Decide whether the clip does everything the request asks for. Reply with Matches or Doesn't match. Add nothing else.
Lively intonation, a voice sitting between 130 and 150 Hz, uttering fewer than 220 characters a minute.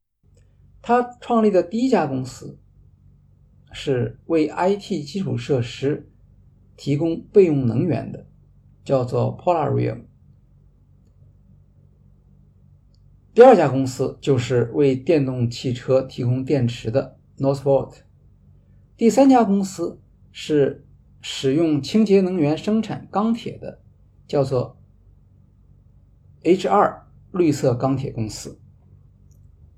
Matches